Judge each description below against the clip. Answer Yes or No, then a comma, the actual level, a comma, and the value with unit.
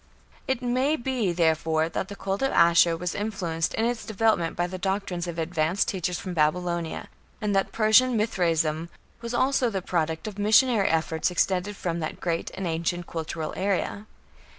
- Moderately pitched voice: Yes, medium, 180 Hz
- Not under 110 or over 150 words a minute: No, average, 170 wpm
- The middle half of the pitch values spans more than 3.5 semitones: Yes, average, 4.4 semitones